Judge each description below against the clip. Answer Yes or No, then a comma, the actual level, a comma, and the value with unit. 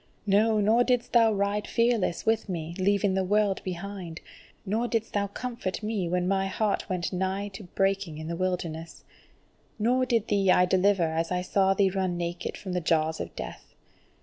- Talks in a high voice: Yes, high, 195 Hz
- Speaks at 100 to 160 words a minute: No, average, 180 wpm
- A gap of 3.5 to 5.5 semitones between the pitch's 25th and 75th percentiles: No, average, 2.8 semitones